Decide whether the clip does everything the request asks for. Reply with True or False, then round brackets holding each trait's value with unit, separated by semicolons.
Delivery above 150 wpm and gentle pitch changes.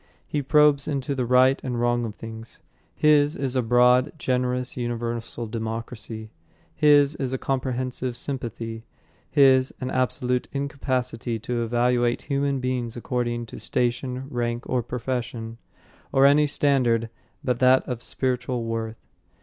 False (135 wpm; 2.0 semitones)